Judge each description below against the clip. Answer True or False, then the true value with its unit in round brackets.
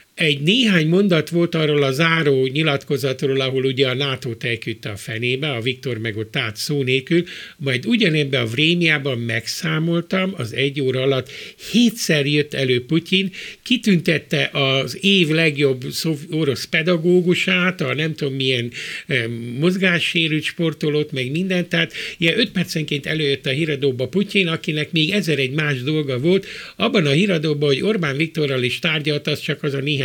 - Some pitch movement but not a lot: True (4.2 semitones)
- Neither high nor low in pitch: True (150 Hz)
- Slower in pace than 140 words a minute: False (155 wpm)